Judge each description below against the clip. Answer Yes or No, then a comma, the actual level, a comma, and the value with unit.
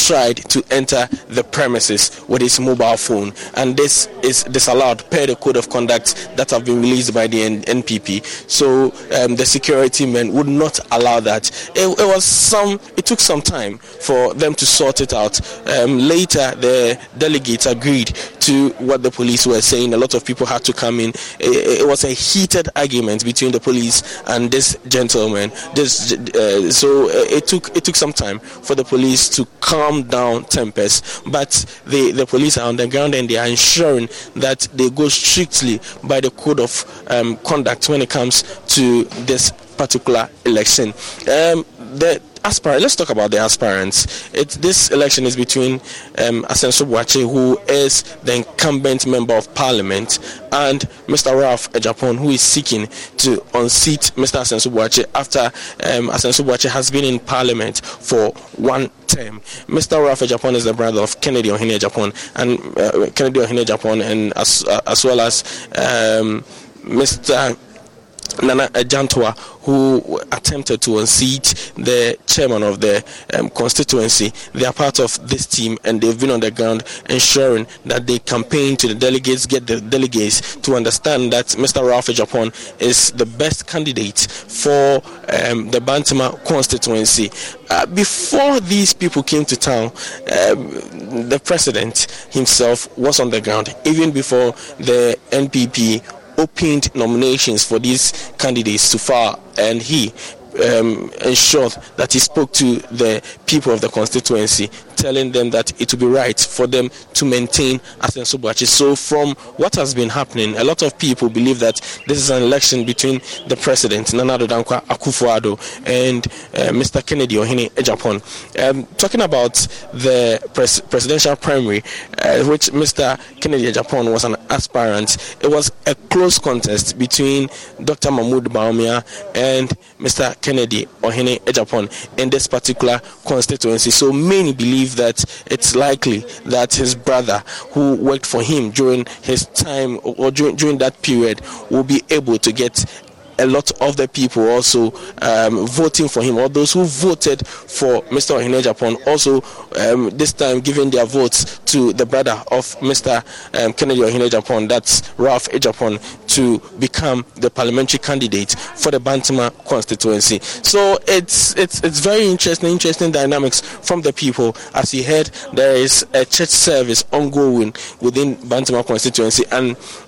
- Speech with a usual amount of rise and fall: Yes, average, 3.0 semitones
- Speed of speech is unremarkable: Yes, average, 155 wpm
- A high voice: No, low, 125 Hz